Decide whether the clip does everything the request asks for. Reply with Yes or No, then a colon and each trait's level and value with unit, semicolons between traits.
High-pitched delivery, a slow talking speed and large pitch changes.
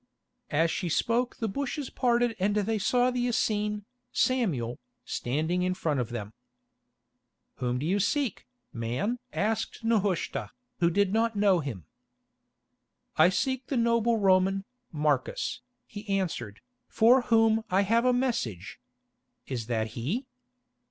Yes: high, 205 Hz; slow, 130 wpm; wide, 7.1 semitones